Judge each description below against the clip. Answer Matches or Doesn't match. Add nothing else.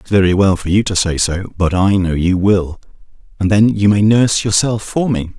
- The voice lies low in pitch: Matches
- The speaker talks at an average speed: Doesn't match